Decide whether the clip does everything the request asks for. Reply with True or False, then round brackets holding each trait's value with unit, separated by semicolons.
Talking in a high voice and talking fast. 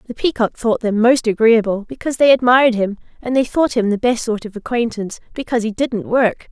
True (230 Hz; 210 wpm)